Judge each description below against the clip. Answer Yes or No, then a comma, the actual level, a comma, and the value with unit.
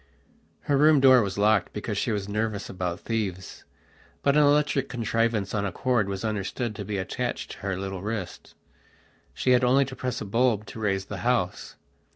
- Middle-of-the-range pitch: No, low, 110 Hz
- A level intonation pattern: No, average, 4.2 semitones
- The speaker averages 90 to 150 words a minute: No, average, 190 wpm